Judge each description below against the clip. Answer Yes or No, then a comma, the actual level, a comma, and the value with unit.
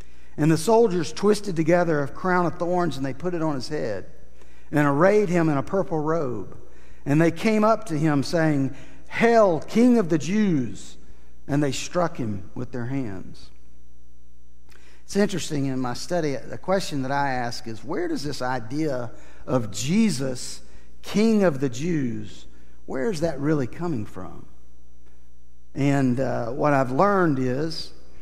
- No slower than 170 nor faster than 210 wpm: No, average, 160 wpm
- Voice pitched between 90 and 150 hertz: Yes, medium, 140 Hz